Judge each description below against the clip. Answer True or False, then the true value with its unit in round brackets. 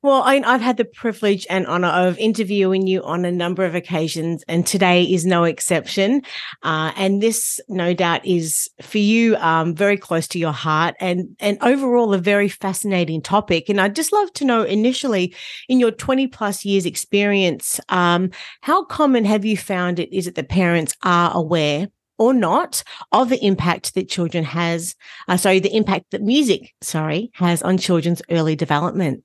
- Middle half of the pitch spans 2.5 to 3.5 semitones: False (3.9 semitones)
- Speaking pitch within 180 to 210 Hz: True (185 Hz)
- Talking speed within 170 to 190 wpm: True (180 wpm)